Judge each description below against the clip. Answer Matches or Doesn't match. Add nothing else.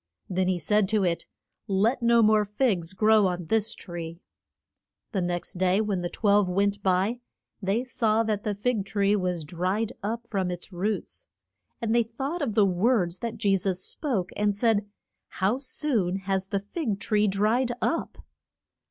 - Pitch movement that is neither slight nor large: Matches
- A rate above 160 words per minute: Matches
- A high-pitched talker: Matches